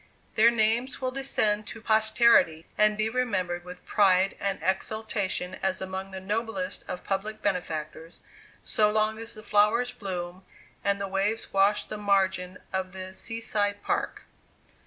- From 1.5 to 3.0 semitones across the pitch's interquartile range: Yes, narrow, 2.6 semitones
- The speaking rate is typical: Yes, average, 150 wpm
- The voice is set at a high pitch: Yes, high, 205 Hz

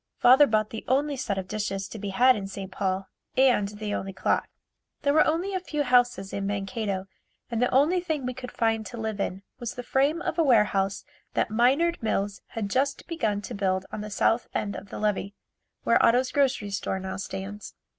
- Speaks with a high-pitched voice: Yes, high, 220 Hz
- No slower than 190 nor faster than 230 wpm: Yes, fast, 205 wpm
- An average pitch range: Yes, average, 4.7 semitones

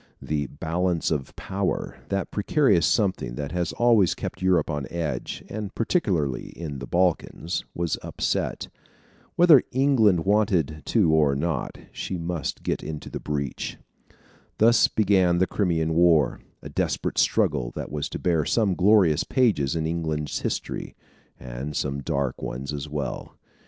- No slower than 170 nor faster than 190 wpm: No, average, 145 wpm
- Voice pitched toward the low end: Yes, very low, 85 Hz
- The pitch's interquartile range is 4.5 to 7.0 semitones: Yes, average, 4.9 semitones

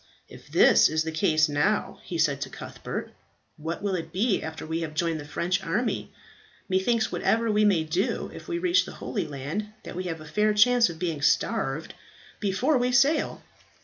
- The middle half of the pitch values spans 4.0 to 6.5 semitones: Yes, average, 5.2 semitones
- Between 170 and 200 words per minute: Yes, average, 190 wpm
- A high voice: No, medium, 180 Hz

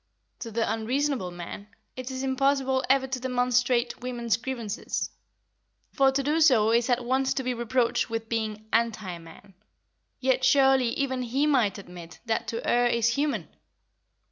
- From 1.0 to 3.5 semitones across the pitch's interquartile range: Yes, average, 2.8 semitones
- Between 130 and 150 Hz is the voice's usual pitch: No, high, 245 Hz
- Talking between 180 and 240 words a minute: No, average, 155 wpm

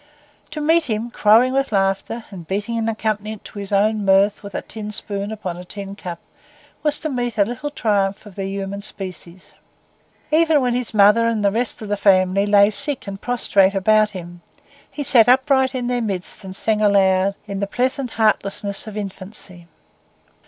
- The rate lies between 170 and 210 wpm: Yes, average, 185 wpm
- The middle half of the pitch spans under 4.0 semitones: Yes, average, 3.2 semitones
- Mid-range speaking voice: No, high, 210 Hz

